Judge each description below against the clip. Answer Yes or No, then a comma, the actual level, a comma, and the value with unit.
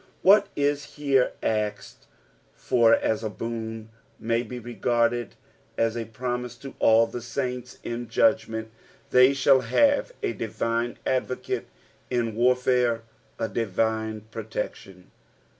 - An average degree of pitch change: No, narrow, 2.1 semitones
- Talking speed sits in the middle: No, slow, 120 wpm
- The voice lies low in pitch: Yes, low, 115 Hz